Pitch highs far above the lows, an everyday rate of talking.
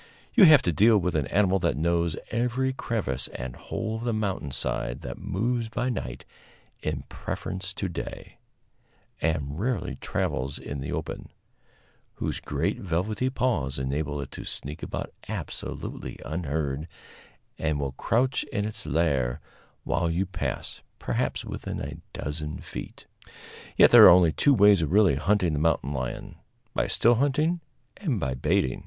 Yes: wide, 7.6 semitones; average, 155 wpm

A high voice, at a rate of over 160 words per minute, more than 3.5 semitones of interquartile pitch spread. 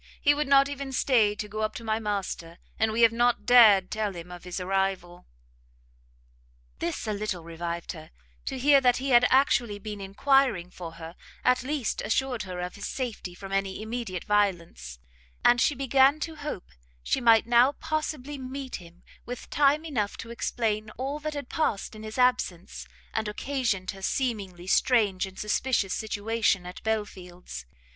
Yes: high, 220 Hz; average, 170 wpm; average, 5.3 semitones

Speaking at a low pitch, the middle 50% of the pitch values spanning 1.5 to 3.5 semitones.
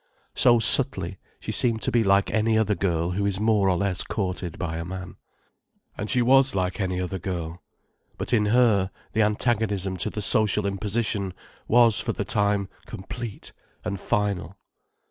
Yes: low, 100 Hz; average, 2.9 semitones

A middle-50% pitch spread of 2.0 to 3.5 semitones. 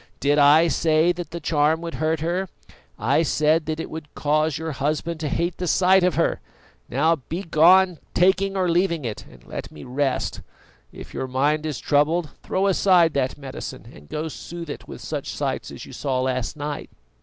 Yes: average, 2.9 semitones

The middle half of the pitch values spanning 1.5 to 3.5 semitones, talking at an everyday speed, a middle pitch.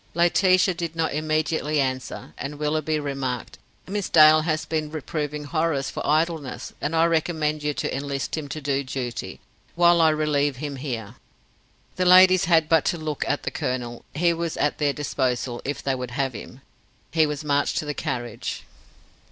Yes: average, 2.8 semitones; average, 175 wpm; medium, 150 Hz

